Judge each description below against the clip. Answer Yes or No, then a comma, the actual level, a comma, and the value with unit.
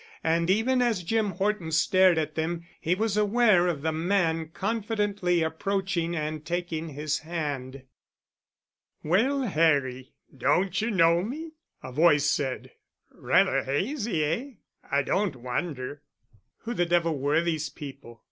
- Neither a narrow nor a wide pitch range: Yes, average, 4.8 semitones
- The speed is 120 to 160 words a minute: Yes, slow, 135 wpm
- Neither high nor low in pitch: Yes, medium, 170 Hz